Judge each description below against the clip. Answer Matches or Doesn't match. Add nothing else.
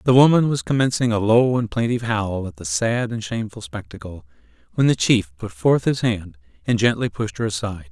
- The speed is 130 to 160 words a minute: Doesn't match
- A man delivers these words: Matches